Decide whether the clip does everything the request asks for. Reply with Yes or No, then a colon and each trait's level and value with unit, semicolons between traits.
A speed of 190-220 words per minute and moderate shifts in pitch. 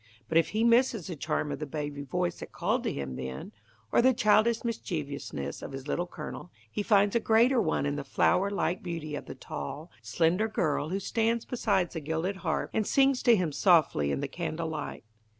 No: fast, 205 wpm; wide, 6.6 semitones